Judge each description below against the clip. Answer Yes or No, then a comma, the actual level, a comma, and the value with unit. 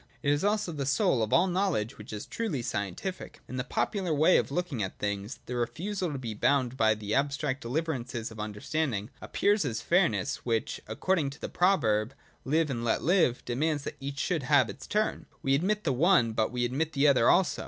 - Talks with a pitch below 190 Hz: Yes, low, 135 Hz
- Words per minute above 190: Yes, fast, 205 wpm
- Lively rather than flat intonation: Yes, wide, 6.2 semitones